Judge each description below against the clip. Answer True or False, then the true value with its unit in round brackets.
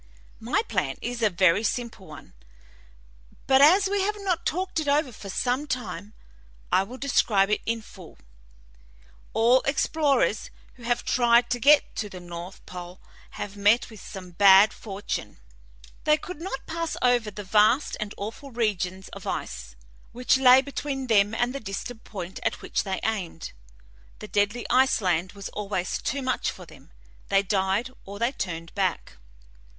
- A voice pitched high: True (220 Hz)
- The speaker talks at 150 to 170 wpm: True (165 wpm)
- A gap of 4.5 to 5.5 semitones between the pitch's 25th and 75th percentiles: True (5.2 semitones)